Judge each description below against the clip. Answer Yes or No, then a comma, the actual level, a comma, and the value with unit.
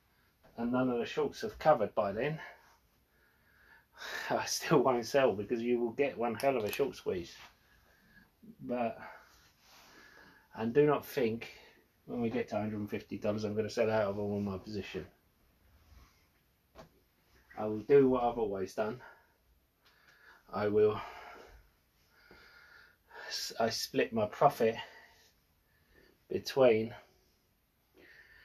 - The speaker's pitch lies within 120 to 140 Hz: No, low, 110 Hz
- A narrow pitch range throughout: No, average, 4.4 semitones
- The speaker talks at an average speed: No, slow, 120 wpm